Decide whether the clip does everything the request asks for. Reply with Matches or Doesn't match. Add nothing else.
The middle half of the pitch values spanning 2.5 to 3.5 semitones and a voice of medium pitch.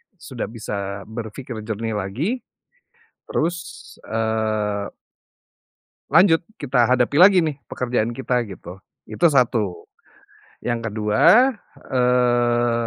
Doesn't match